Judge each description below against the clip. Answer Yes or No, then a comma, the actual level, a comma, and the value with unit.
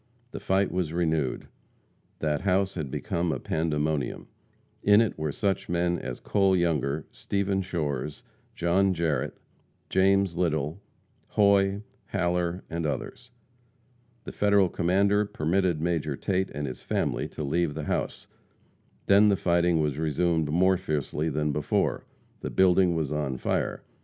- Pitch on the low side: Yes, very low, 85 Hz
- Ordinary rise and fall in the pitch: Yes, average, 3.9 semitones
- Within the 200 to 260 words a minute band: No, slow, 135 wpm